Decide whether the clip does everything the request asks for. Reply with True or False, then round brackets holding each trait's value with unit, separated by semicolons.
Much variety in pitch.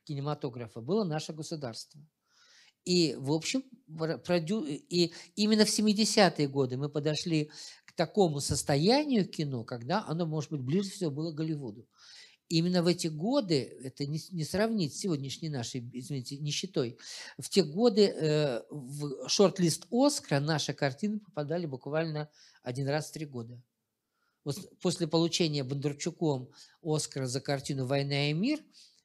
False (4.0 semitones)